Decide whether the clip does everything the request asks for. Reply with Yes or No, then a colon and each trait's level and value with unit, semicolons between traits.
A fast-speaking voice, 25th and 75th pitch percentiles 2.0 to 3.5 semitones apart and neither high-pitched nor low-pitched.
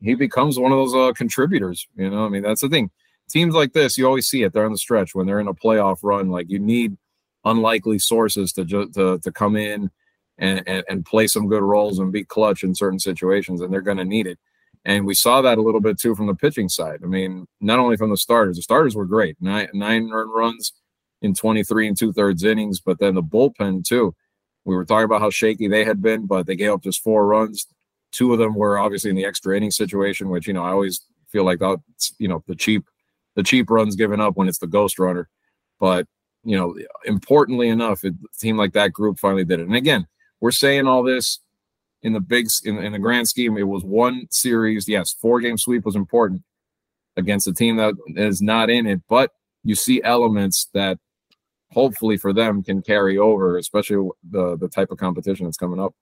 No: fast, 225 wpm; narrow, 2.6 semitones; low, 105 Hz